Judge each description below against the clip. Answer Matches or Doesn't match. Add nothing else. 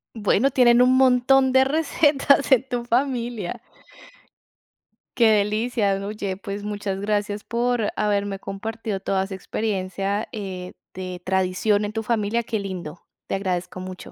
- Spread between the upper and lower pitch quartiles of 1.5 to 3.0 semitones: Doesn't match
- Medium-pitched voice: Doesn't match